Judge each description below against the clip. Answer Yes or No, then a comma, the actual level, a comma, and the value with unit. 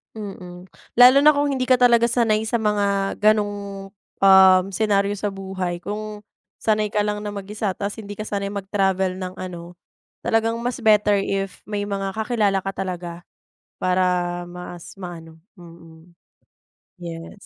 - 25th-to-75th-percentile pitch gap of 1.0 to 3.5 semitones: Yes, narrow, 2.5 semitones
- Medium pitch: No, high, 200 Hz